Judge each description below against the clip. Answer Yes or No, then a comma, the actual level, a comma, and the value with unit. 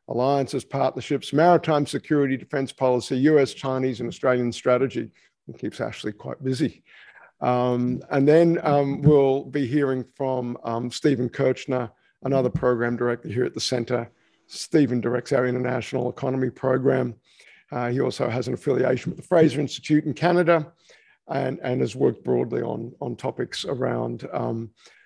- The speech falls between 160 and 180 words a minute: No, average, 150 wpm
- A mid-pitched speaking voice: No, low, 130 Hz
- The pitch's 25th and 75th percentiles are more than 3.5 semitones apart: No, average, 2.7 semitones